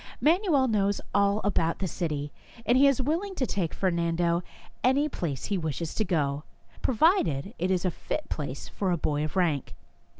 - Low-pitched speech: No, medium, 185 Hz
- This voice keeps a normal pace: Yes, average, 180 wpm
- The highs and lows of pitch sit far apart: Yes, wide, 7.9 semitones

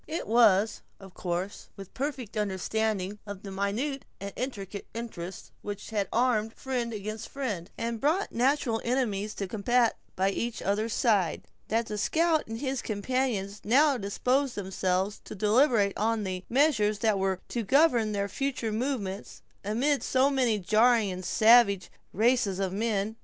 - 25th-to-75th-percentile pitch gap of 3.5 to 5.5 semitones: Yes, average, 3.9 semitones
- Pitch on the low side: No, high, 220 Hz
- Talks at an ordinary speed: Yes, average, 155 wpm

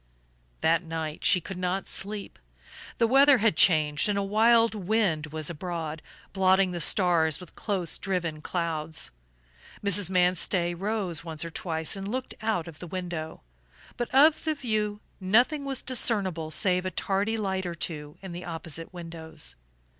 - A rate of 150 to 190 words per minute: Yes, average, 155 wpm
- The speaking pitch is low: No, medium, 180 Hz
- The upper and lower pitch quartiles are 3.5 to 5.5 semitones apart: Yes, average, 4.2 semitones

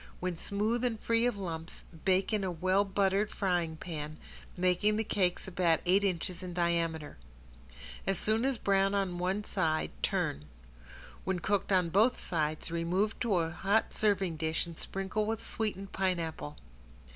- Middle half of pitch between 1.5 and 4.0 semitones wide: Yes, average, 3.2 semitones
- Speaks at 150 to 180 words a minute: Yes, average, 155 wpm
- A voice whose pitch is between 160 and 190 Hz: Yes, medium, 185 Hz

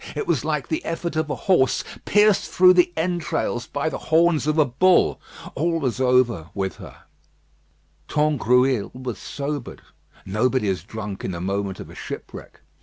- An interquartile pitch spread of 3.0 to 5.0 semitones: No, wide, 5.6 semitones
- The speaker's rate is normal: Yes, average, 165 wpm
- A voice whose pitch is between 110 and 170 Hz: Yes, medium, 140 Hz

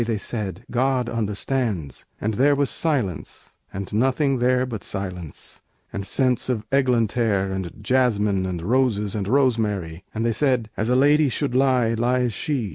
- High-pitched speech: No, low, 115 Hz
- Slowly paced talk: No, average, 155 wpm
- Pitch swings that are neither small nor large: Yes, average, 4.3 semitones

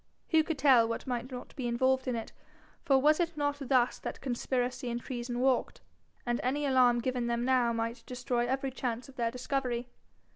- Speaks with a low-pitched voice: No, very high, 250 Hz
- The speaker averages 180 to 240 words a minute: Yes, average, 190 wpm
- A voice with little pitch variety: Yes, narrow, 1.9 semitones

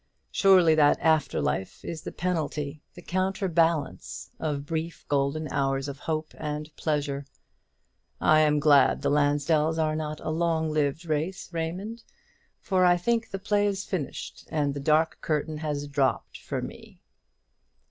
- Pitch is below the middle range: No, medium, 155 Hz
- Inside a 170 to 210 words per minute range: No, average, 150 wpm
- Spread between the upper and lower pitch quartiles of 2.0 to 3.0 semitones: Yes, narrow, 2.6 semitones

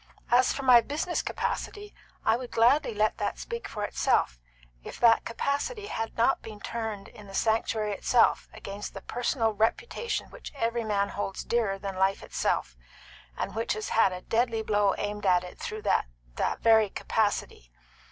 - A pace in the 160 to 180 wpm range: Yes, average, 170 wpm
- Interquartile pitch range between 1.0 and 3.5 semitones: Yes, average, 3.1 semitones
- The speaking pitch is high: Yes, high, 225 Hz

